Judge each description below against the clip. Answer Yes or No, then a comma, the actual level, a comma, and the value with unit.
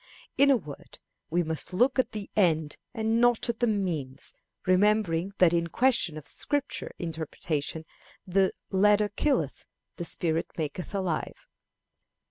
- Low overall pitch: No, medium, 185 Hz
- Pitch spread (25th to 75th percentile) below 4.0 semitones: No, average, 5.3 semitones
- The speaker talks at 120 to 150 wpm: Yes, slow, 135 wpm